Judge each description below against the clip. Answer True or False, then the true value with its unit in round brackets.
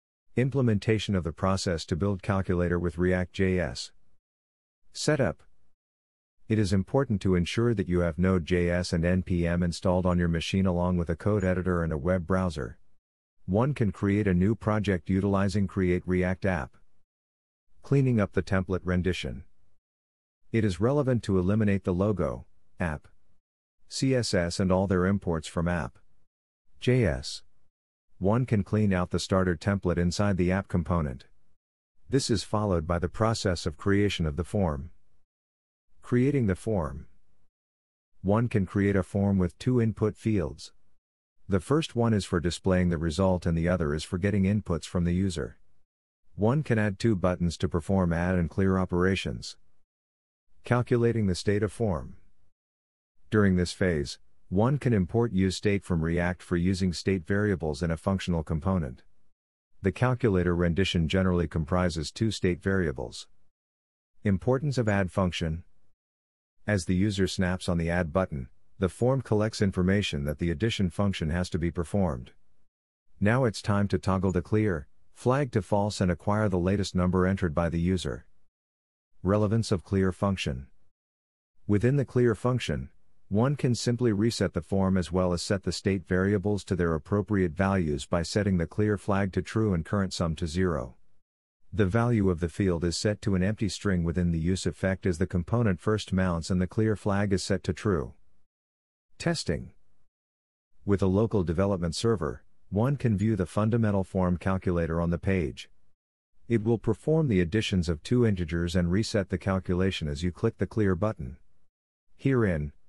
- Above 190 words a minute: False (160 wpm)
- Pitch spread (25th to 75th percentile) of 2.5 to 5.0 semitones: True (3.3 semitones)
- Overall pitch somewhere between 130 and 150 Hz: False (95 Hz)